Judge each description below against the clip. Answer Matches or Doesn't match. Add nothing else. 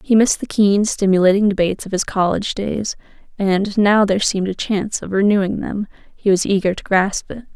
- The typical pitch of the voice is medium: Doesn't match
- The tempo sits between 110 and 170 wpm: Doesn't match